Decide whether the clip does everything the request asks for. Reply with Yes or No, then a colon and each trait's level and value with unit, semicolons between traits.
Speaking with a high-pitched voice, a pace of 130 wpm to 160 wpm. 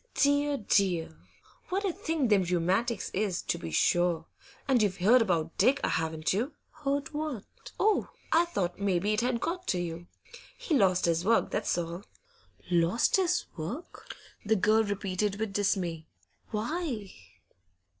Yes: high, 205 Hz; average, 145 wpm